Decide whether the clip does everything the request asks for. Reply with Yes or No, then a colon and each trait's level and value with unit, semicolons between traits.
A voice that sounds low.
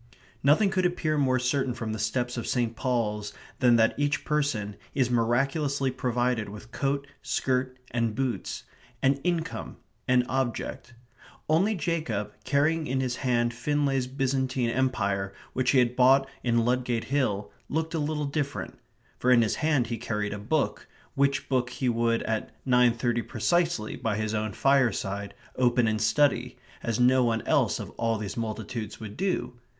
Yes: low, 125 Hz